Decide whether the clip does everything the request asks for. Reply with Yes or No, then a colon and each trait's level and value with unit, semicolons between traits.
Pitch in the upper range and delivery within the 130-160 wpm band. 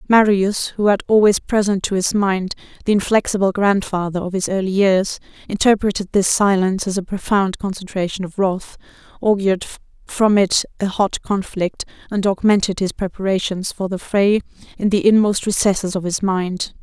Yes: high, 195 Hz; average, 155 wpm